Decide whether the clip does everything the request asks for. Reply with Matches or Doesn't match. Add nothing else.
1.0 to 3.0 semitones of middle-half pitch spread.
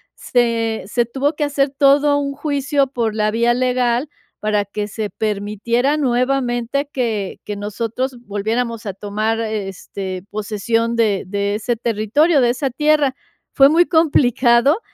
Doesn't match